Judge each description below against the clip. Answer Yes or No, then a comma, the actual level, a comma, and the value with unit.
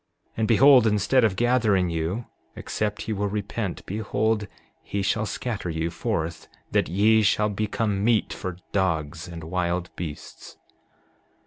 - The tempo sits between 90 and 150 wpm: Yes, average, 140 wpm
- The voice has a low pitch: Yes, low, 100 Hz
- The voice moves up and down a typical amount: Yes, average, 3.8 semitones